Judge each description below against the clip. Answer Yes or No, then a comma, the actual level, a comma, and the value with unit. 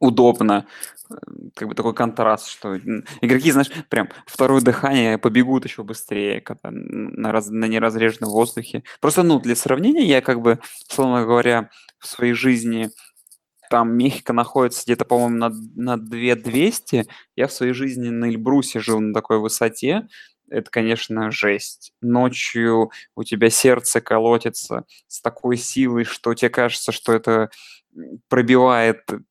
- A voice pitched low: Yes, low, 120 Hz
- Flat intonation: Yes, narrow, 2.0 semitones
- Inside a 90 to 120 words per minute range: No, average, 135 wpm